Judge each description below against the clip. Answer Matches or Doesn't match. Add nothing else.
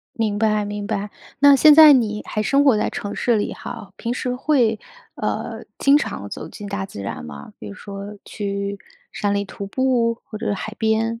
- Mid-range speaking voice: Doesn't match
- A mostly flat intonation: Doesn't match